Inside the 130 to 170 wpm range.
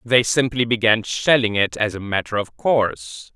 No: average, 180 wpm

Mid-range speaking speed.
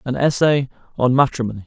Yes: average, 145 wpm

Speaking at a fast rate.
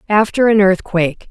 No: average, 140 wpm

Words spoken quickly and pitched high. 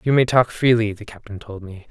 No: fast, 250 wpm; low, 110 Hz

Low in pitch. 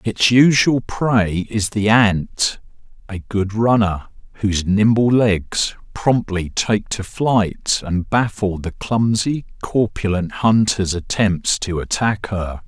Yes: low, 105 Hz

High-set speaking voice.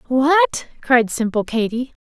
Yes: high, 245 Hz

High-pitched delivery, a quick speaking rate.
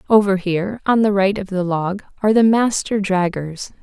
No: high, 195 Hz; average, 190 wpm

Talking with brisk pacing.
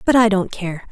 Yes: fast, 260 wpm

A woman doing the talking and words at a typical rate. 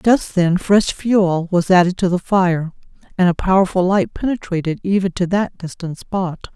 Yes: female; average, 175 wpm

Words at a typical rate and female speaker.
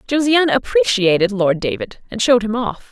Yes: average, 165 wpm; female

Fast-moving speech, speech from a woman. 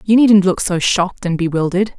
Yes: fast, 210 wpm; female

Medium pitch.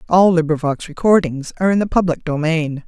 Yes: medium, 165 Hz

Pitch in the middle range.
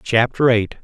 No: low, 115 Hz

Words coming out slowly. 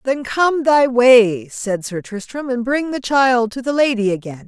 No: average, 200 wpm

